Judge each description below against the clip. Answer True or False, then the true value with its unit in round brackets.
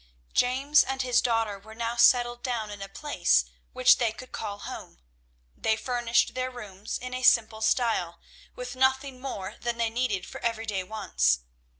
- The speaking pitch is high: True (235 Hz)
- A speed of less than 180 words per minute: True (170 wpm)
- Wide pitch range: False (2.9 semitones)